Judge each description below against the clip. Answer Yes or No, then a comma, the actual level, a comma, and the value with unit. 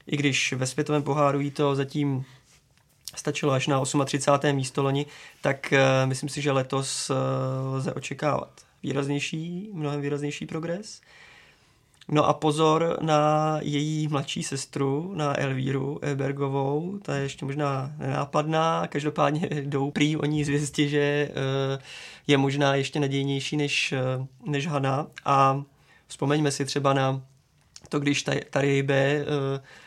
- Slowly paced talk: No, average, 130 wpm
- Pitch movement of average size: No, narrow, 1.5 semitones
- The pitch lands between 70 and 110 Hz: No, medium, 140 Hz